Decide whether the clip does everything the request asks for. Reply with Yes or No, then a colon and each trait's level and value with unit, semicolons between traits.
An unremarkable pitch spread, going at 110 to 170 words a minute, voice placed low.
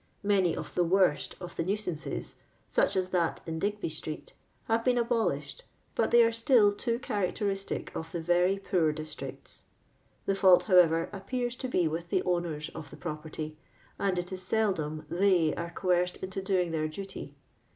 No: average, 3.6 semitones; average, 165 wpm; medium, 185 Hz